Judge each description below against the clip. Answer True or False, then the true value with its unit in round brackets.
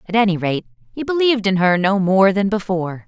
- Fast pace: True (215 wpm)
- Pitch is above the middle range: True (195 Hz)